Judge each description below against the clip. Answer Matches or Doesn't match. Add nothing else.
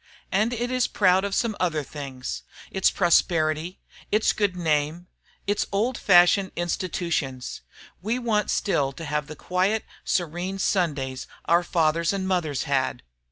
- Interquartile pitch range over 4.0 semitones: Matches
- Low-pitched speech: Doesn't match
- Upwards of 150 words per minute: Doesn't match